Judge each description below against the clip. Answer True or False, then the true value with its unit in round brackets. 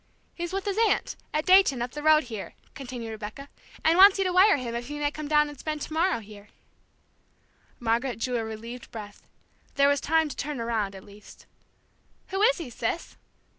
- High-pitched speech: True (280 Hz)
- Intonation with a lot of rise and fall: True (5.7 semitones)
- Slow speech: False (195 wpm)